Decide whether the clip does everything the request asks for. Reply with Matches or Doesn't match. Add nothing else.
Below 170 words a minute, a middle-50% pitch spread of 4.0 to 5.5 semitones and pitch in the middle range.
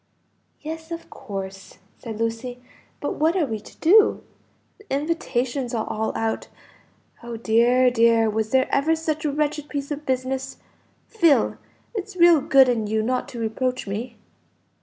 Doesn't match